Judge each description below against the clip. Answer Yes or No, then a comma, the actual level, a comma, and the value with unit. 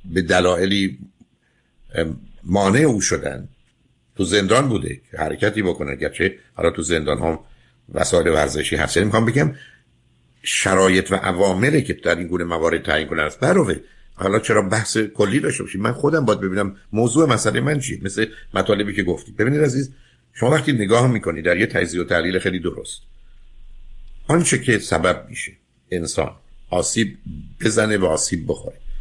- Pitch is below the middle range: Yes, low, 100 Hz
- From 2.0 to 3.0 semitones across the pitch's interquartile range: No, average, 5.1 semitones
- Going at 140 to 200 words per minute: Yes, average, 150 wpm